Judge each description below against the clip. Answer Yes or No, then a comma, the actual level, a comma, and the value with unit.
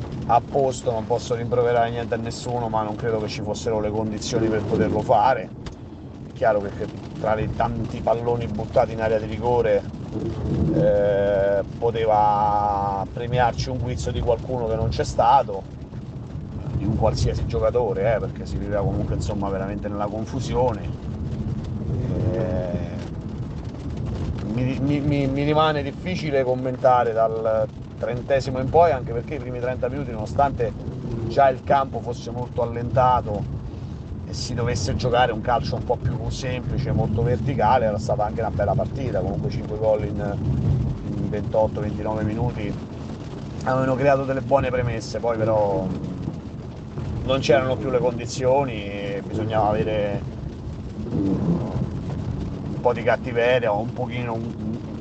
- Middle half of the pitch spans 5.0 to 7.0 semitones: No, average, 2.8 semitones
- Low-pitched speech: Yes, low, 115 Hz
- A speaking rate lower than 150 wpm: Yes, average, 140 wpm